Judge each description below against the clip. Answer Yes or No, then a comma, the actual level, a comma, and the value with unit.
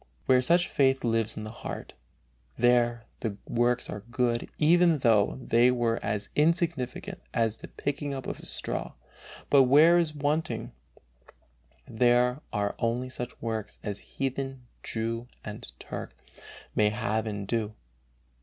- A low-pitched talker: Yes, low, 120 Hz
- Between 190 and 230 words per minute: No, average, 145 wpm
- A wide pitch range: No, average, 3.3 semitones